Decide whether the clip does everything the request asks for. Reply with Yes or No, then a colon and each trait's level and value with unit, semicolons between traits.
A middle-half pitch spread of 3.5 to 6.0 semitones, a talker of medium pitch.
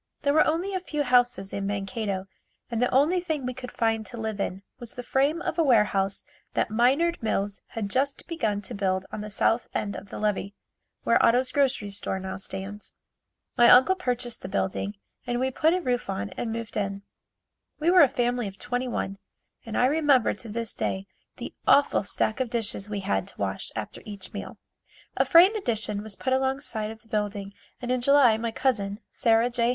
No: average, 4.4 semitones; high, 230 Hz